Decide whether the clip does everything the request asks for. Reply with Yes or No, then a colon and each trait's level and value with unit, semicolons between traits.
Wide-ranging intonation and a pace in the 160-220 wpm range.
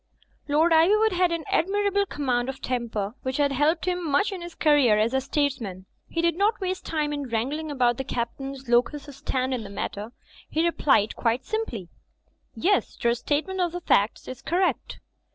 Yes: wide, 6.1 semitones; average, 185 wpm